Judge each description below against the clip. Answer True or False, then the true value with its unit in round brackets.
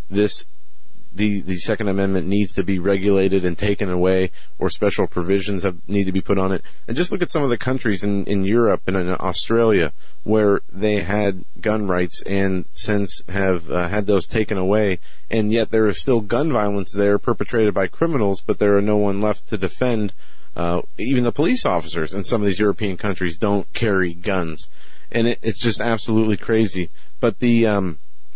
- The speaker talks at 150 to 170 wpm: False (195 wpm)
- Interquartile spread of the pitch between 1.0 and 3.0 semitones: True (2.4 semitones)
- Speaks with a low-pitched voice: True (100 Hz)